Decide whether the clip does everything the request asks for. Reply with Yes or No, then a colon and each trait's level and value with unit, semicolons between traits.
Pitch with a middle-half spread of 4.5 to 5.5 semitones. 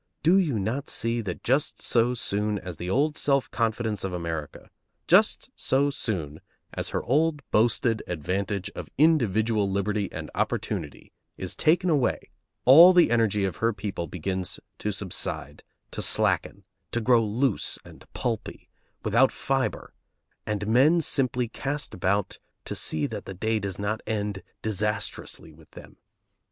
Yes: average, 5.1 semitones